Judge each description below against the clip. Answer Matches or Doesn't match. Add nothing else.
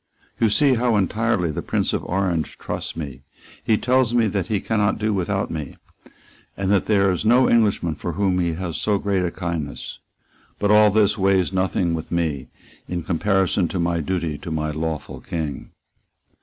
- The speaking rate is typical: Matches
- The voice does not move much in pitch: Doesn't match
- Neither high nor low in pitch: Doesn't match